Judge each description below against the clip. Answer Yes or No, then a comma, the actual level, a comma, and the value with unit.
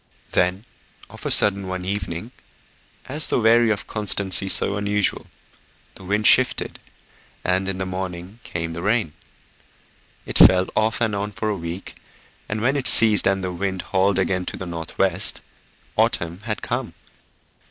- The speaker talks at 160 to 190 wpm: Yes, average, 165 wpm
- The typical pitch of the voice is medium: No, very low, 95 Hz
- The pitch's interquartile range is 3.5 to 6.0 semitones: No, narrow, 2.5 semitones